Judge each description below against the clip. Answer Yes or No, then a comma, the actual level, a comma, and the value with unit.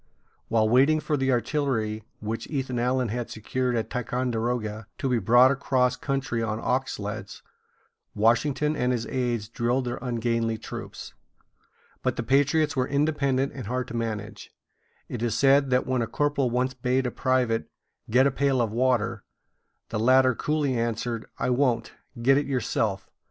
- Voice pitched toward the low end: Yes, low, 125 Hz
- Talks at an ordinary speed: Yes, average, 160 wpm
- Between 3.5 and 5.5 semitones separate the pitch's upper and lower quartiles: No, narrow, 2.6 semitones